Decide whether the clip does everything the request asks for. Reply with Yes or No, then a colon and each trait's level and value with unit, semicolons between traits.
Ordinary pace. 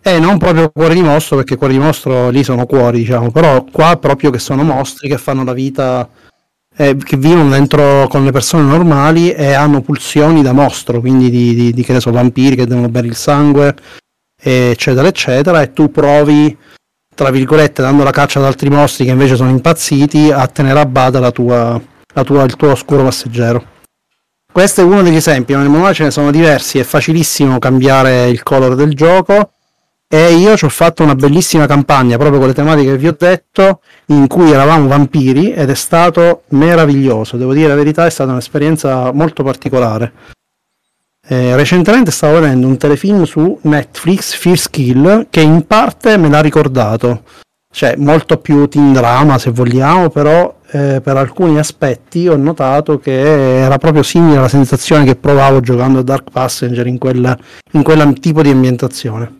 No: fast, 180 wpm